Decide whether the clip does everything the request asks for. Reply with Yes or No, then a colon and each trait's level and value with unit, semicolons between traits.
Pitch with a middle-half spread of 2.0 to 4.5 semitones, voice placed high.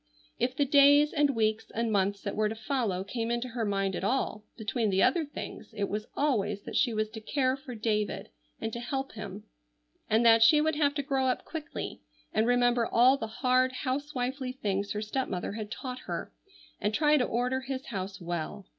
Yes: average, 4.0 semitones; high, 235 Hz